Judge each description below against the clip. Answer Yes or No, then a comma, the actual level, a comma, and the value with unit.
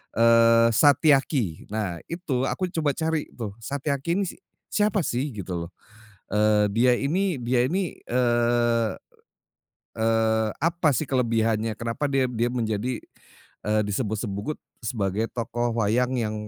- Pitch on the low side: Yes, low, 120 Hz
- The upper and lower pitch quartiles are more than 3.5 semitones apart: Yes, average, 4.0 semitones